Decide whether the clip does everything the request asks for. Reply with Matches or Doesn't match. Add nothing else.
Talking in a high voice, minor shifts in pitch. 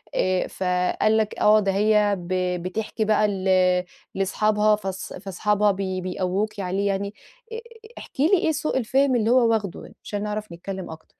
Matches